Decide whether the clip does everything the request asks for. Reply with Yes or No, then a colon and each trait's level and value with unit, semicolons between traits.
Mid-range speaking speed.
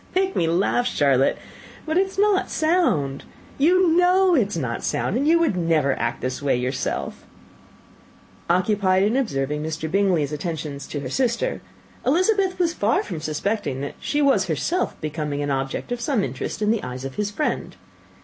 Yes: average, 185 wpm